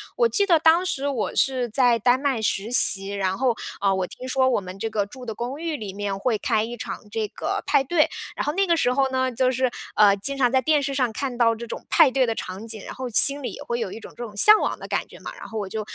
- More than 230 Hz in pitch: Yes, high, 245 Hz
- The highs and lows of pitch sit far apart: No, average, 4.0 semitones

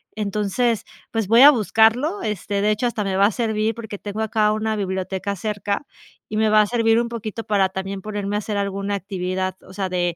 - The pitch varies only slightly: Yes, narrow, 2.0 semitones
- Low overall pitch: No, high, 210 Hz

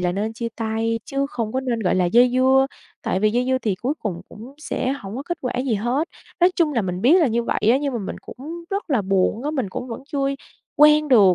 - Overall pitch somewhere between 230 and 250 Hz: Yes, high, 245 Hz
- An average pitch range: Yes, average, 4.4 semitones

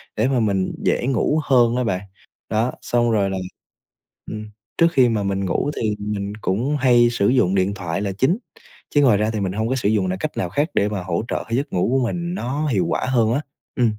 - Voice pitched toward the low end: Yes, low, 110 Hz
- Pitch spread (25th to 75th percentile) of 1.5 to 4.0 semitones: No, average, 4.4 semitones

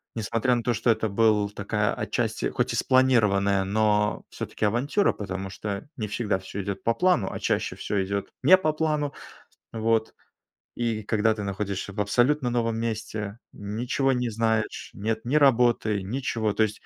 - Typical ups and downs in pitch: Yes, average, 3.0 semitones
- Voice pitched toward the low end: Yes, low, 110 Hz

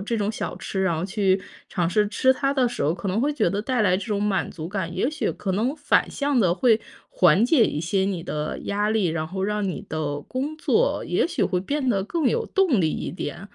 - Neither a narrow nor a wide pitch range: No, wide, 5.8 semitones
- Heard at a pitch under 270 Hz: Yes, high, 205 Hz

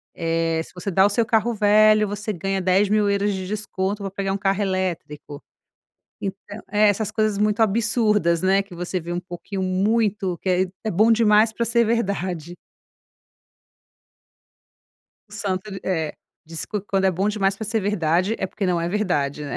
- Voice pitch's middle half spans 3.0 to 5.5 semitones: No, narrow, 2.5 semitones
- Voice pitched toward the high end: Yes, high, 195 Hz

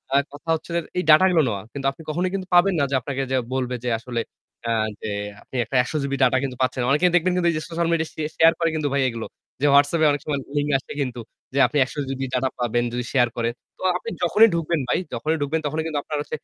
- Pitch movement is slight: No, average, 4.3 semitones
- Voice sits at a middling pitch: Yes, medium, 145 Hz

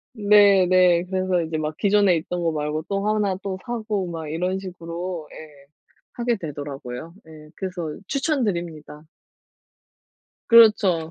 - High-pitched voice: No, medium, 180 Hz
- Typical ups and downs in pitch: Yes, average, 4.2 semitones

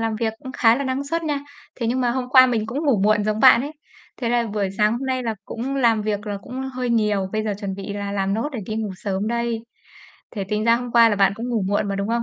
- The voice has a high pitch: Yes, high, 225 Hz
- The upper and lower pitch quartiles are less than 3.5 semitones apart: Yes, average, 3.1 semitones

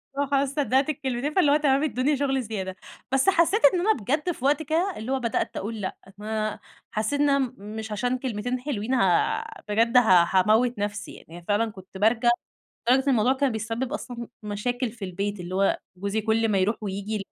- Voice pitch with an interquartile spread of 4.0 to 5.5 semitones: Yes, average, 4.7 semitones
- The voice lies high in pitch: Yes, high, 235 Hz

